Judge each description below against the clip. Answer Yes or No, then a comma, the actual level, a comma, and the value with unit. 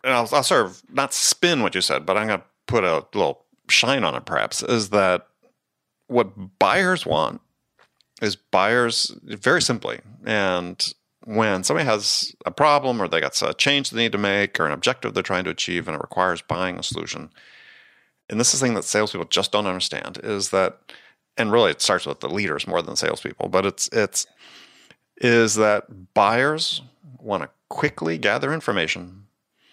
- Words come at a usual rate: Yes, average, 185 wpm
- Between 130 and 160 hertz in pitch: No, low, 105 Hz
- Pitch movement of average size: Yes, average, 4.2 semitones